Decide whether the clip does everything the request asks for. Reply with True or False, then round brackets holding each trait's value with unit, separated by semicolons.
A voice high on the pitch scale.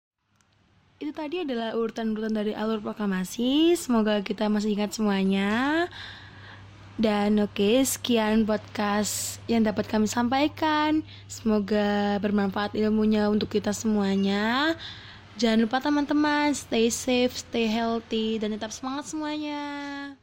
True (220 Hz)